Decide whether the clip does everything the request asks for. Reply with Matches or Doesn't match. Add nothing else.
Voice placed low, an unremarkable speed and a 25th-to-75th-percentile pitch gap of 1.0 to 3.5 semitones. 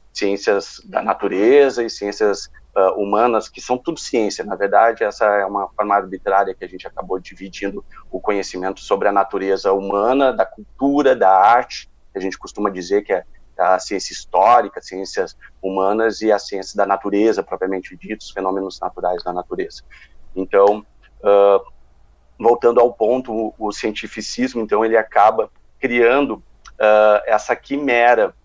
Matches